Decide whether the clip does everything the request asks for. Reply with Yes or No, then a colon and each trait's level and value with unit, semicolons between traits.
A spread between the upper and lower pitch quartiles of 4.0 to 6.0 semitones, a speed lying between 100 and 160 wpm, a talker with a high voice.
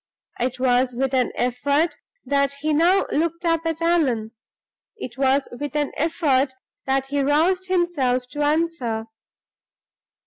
Yes: average, 4.3 semitones; slow, 135 wpm; very high, 285 Hz